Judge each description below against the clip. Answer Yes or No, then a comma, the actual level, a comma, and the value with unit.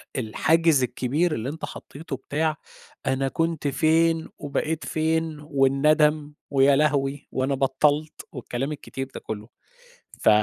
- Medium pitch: Yes, medium, 145 Hz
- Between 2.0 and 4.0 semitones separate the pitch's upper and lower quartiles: Yes, average, 2.7 semitones